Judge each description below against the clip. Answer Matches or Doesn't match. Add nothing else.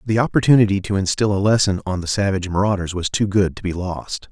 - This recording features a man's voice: Matches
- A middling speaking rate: Doesn't match